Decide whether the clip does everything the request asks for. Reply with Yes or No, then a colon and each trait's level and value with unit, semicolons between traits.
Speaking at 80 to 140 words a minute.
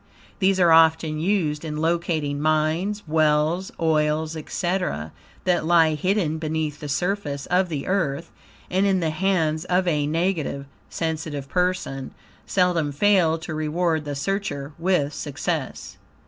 Yes: slow, 135 wpm